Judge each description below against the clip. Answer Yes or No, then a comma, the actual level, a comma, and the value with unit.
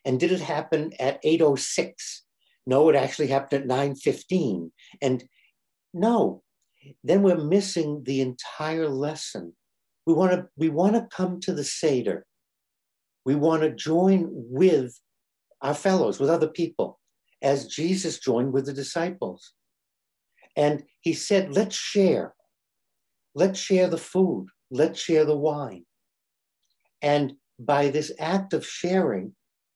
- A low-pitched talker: No, medium, 155 Hz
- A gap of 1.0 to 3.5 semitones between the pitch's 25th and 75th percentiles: No, average, 4.5 semitones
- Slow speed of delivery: Yes, slow, 125 wpm